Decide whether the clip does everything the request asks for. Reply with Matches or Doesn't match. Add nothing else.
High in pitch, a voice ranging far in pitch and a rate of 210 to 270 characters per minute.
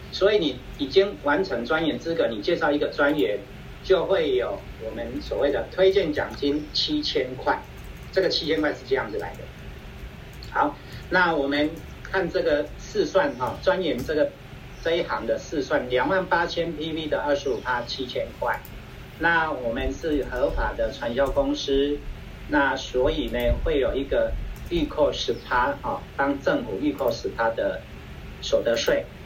Doesn't match